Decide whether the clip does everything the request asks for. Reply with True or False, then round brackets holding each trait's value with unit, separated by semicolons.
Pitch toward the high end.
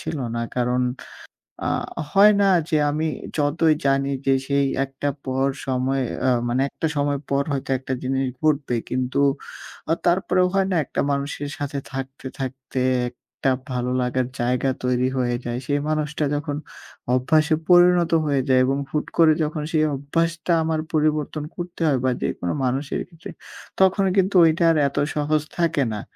False (145 Hz)